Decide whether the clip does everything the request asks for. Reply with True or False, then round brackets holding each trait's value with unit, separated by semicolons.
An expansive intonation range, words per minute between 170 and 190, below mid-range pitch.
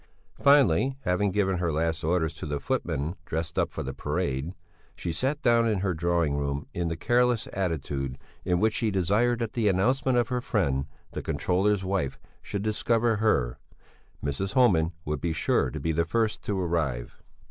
True (5.7 semitones; 180 wpm; 90 Hz)